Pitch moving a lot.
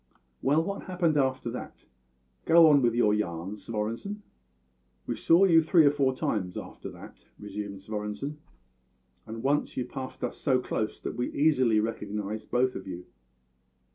Yes: wide, 5.8 semitones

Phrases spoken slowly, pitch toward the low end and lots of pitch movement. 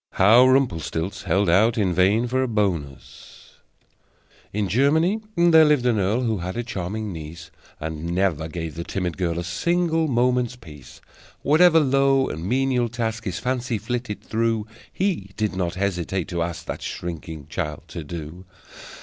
No: average, 160 wpm; low, 105 Hz; wide, 6.5 semitones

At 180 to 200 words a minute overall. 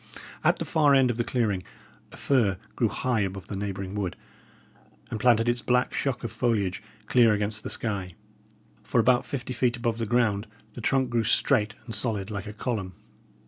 Yes: average, 185 wpm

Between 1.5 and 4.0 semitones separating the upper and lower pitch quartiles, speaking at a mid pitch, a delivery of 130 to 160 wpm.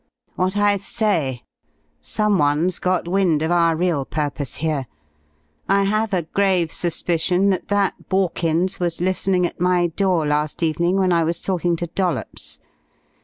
Yes: average, 2.9 semitones; medium, 175 Hz; average, 145 wpm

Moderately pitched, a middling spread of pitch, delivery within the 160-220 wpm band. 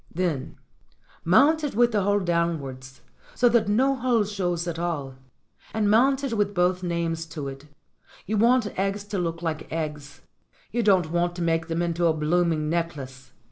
Yes: medium, 175 Hz; average, 4.2 semitones; average, 175 wpm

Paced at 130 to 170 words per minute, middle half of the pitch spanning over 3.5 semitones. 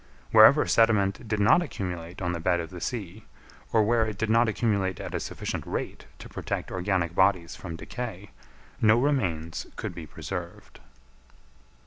Yes: average, 160 wpm; average, 4.1 semitones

